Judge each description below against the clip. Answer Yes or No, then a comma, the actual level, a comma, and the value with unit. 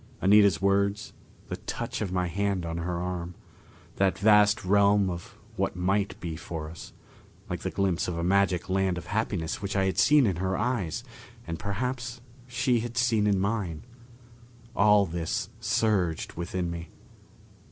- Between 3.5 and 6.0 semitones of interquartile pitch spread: No, average, 3.0 semitones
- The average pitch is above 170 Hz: No, very low, 95 Hz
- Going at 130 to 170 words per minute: Yes, average, 160 wpm